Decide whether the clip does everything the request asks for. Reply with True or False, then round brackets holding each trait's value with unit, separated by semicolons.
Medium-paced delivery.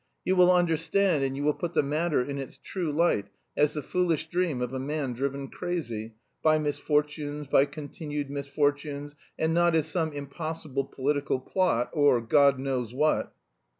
True (165 wpm)